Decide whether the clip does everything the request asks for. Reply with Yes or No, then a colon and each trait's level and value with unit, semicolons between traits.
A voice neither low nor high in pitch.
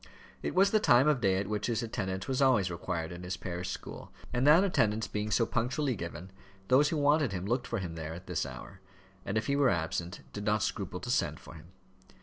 No: low, 105 Hz